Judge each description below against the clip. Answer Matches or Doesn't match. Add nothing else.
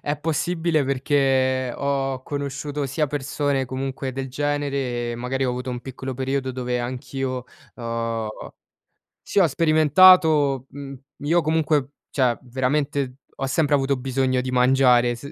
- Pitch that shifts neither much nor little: Doesn't match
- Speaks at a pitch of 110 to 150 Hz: Matches